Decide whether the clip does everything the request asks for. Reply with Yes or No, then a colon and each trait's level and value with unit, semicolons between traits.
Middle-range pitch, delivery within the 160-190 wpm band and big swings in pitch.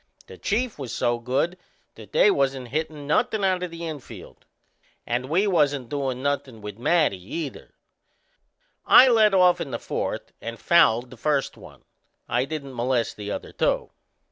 Yes: medium, 145 Hz; average, 165 wpm; wide, 5.8 semitones